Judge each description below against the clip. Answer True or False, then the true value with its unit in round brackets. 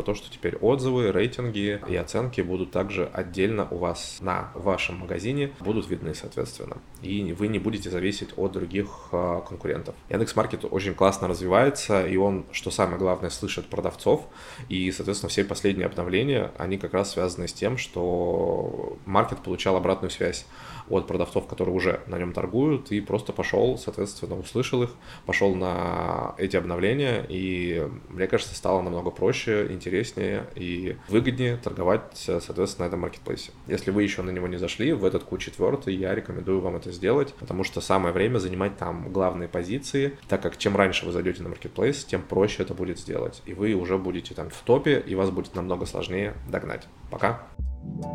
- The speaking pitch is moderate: False (95 Hz)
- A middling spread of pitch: False (2.3 semitones)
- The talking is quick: True (170 wpm)